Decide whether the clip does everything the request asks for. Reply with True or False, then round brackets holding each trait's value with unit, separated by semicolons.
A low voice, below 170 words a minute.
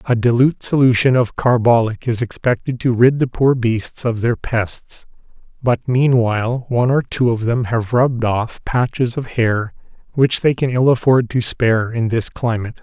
False (120 Hz; 180 wpm)